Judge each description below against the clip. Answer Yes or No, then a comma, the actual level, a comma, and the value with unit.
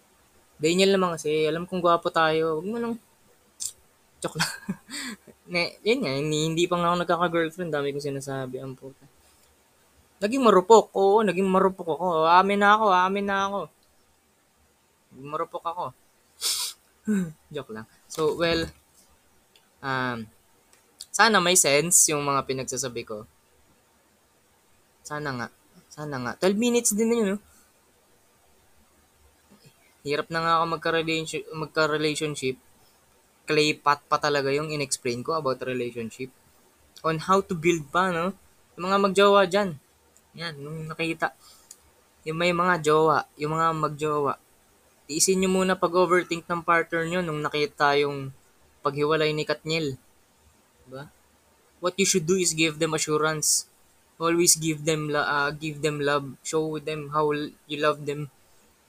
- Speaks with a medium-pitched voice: Yes, medium, 155 Hz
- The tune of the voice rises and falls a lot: No, average, 3.8 semitones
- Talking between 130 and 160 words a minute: Yes, average, 140 wpm